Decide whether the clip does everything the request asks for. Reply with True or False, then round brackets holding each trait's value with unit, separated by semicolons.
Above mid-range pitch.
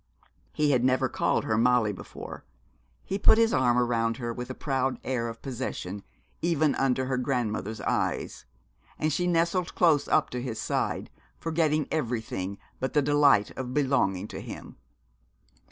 False (130 Hz)